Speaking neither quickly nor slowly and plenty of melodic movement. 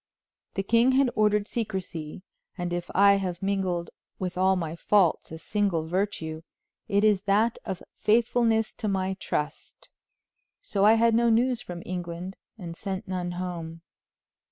No: average, 150 wpm; average, 3.4 semitones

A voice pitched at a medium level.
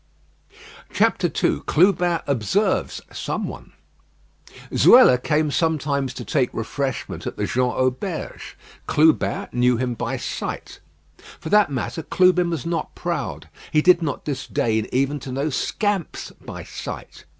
Yes: medium, 145 Hz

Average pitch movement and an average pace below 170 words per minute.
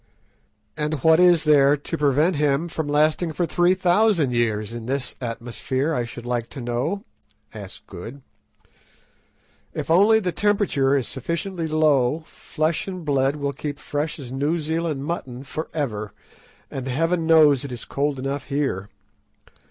Yes: average, 4.0 semitones; average, 150 wpm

